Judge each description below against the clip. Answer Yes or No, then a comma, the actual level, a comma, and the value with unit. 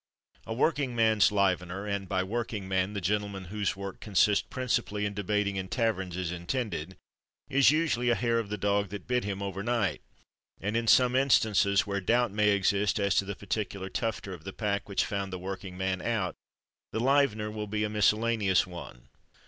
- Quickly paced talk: No, average, 190 wpm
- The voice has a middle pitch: No, low, 100 Hz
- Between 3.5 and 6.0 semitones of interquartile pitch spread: No, average, 2.7 semitones